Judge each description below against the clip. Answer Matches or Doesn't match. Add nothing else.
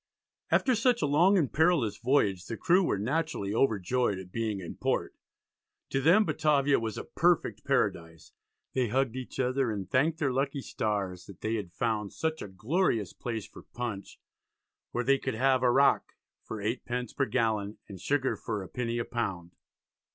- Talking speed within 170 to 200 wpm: Matches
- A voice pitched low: Matches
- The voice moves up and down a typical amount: Matches